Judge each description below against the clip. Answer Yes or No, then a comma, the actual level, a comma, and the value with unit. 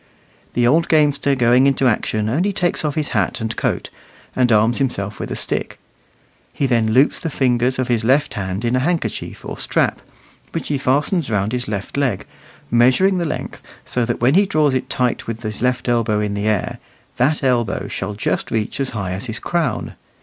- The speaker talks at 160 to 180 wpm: No, average, 200 wpm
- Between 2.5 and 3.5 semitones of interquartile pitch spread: No, average, 4.2 semitones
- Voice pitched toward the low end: Yes, low, 125 Hz